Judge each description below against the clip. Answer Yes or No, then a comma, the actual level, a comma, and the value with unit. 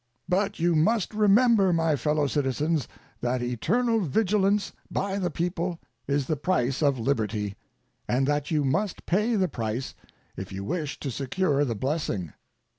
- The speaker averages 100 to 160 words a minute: Yes, average, 150 wpm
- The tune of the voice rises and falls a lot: Yes, wide, 6.5 semitones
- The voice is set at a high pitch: No, medium, 155 Hz